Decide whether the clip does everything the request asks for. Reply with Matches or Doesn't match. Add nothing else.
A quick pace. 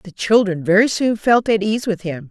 Matches